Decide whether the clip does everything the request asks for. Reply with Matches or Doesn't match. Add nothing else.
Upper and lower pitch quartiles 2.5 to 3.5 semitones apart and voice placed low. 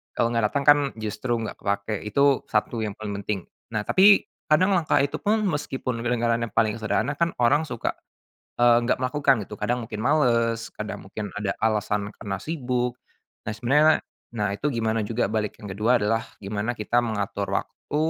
Doesn't match